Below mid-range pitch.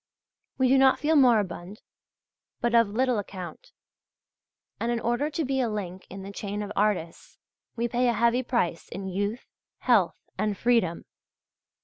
No: high, 225 Hz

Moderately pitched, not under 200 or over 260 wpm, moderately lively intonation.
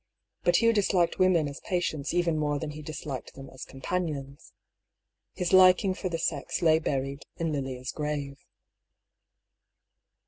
No: medium, 155 Hz; average, 140 wpm; average, 4.1 semitones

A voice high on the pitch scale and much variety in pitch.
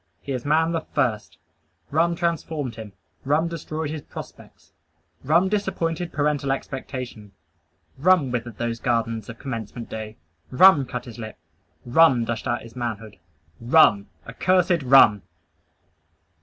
No: low, 130 Hz; wide, 5.8 semitones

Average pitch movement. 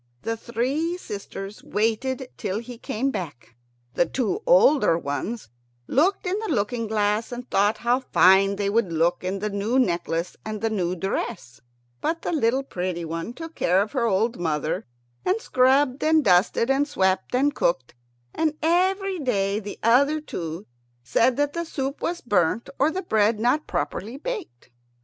No: wide, 6.7 semitones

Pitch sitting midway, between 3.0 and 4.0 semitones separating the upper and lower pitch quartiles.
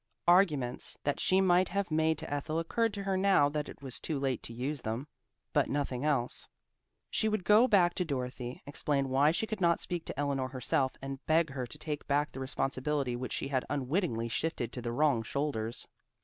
No: medium, 145 Hz; average, 4.4 semitones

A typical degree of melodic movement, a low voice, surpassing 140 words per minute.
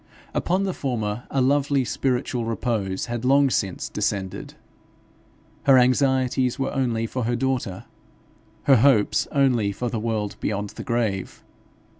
No: average, 3.7 semitones; low, 120 Hz; slow, 135 wpm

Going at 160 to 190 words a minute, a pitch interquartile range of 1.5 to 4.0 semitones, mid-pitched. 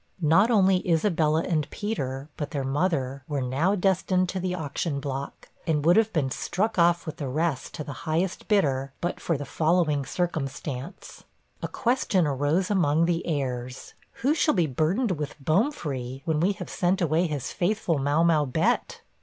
No: average, 170 wpm; average, 4.4 semitones; medium, 160 Hz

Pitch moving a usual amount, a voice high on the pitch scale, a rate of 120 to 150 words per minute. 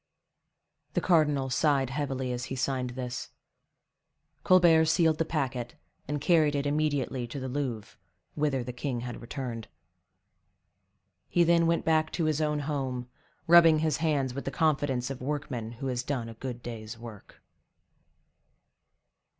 No: average, 3.7 semitones; low, 135 Hz; average, 145 wpm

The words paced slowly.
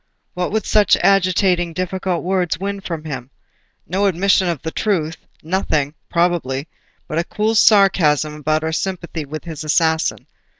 No: average, 145 wpm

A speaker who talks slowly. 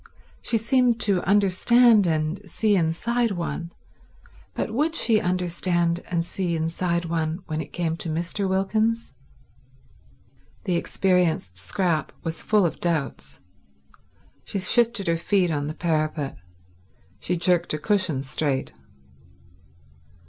Yes: slow, 120 wpm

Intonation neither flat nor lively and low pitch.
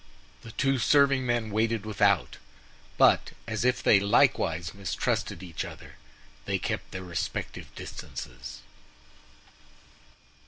Yes: average, 4.3 semitones; low, 105 Hz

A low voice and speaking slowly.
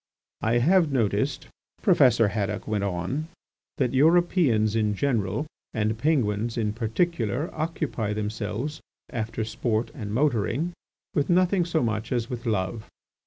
Yes: low, 115 Hz; slow, 125 wpm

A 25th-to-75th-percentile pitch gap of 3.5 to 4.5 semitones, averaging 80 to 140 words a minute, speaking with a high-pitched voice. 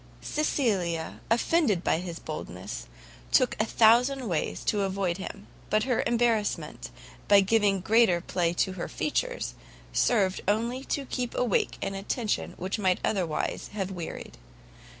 Yes: average, 4.1 semitones; slow, 135 wpm; high, 205 Hz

